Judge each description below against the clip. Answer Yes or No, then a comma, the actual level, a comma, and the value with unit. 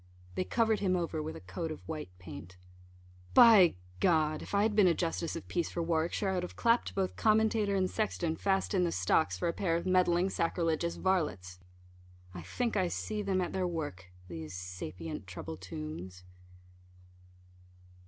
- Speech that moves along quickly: No, average, 175 wpm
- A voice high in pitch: No, medium, 170 Hz